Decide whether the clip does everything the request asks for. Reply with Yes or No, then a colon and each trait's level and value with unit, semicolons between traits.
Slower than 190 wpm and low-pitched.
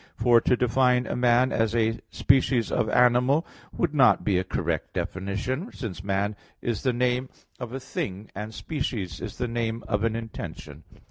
Yes: average, 175 wpm; low, 115 Hz